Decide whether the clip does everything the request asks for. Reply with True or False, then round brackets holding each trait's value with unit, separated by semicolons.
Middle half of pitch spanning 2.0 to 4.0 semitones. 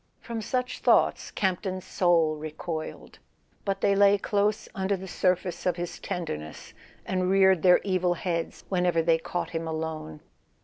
True (2.8 semitones)